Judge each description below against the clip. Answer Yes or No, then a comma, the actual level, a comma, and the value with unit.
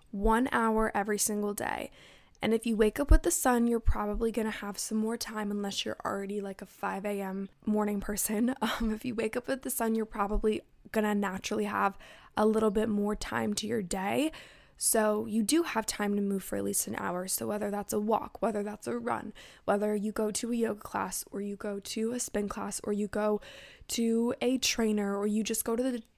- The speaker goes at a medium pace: No, fast, 220 wpm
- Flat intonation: Yes, narrow, 1.8 semitones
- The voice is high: Yes, high, 215 Hz